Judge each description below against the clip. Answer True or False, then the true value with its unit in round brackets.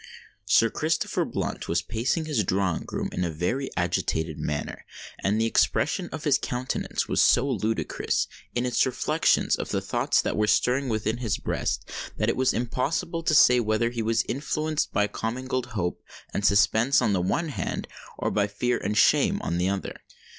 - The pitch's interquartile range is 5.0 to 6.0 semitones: False (4.3 semitones)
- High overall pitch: False (115 Hz)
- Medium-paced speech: True (180 wpm)